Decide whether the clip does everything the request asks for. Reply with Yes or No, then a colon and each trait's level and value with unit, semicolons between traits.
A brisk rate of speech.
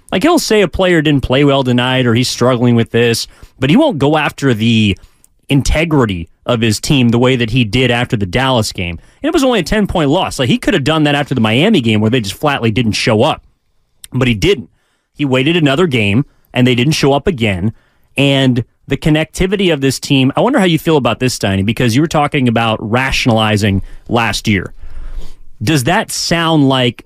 Yes: fast, 215 wpm